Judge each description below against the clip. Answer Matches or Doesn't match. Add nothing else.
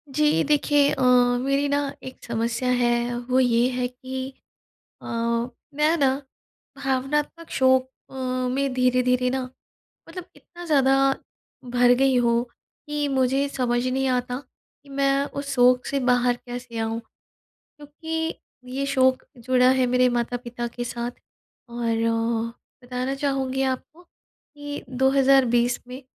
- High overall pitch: Matches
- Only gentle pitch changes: Matches